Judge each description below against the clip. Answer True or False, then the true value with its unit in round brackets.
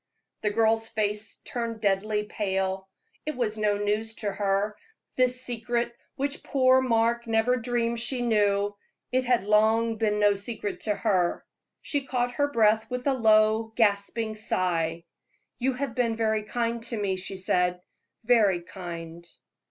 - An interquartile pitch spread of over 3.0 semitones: False (2.7 semitones)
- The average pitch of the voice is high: True (220 Hz)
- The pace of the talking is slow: False (150 wpm)